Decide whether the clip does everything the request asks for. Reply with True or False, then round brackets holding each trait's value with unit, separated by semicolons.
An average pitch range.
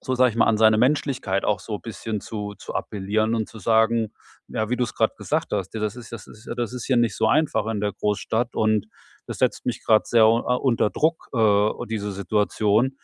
False (2.2 semitones)